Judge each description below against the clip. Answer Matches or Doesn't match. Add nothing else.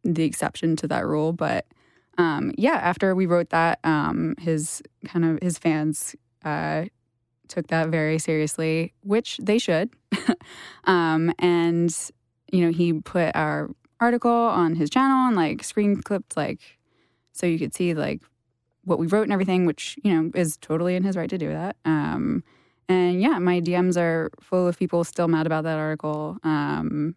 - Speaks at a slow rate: Doesn't match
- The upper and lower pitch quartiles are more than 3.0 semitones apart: Doesn't match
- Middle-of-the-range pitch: Matches